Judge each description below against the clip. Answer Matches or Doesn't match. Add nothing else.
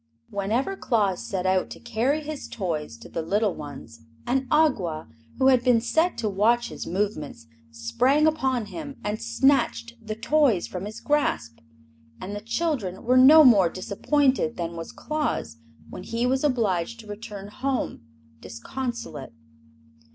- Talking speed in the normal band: Matches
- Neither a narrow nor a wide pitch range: Doesn't match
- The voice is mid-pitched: Doesn't match